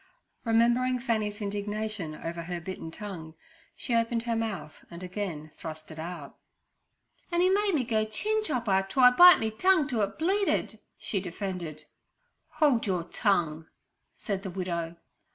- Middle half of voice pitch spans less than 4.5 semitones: No, wide, 5.6 semitones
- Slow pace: No, average, 155 wpm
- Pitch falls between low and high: No, high, 205 Hz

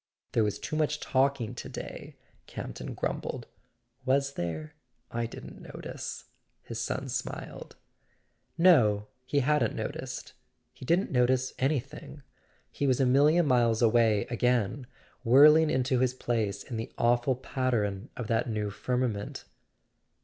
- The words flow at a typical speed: No, slow, 130 wpm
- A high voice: No, low, 125 Hz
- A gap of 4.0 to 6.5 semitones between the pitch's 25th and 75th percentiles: No, average, 3.4 semitones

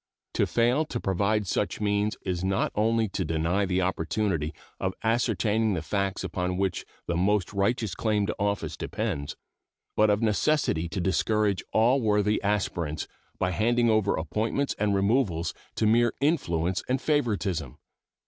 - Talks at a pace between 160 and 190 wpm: No, average, 150 wpm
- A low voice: Yes, low, 100 Hz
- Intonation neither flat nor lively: Yes, average, 3.3 semitones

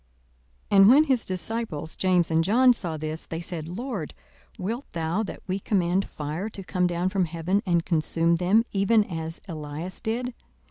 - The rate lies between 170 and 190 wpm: Yes, average, 175 wpm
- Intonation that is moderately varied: Yes, average, 4.1 semitones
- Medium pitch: Yes, medium, 180 Hz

